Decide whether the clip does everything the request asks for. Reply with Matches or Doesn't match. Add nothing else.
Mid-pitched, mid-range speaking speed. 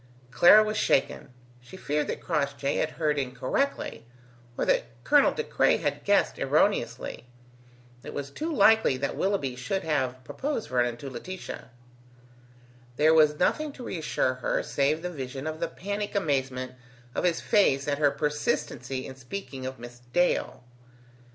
Matches